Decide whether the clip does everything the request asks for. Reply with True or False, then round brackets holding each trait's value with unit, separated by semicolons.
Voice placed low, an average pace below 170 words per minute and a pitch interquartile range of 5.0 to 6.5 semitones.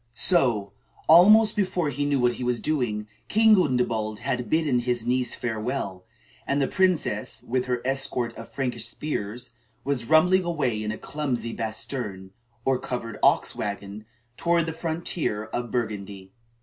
True (125 Hz; 150 wpm; 5.6 semitones)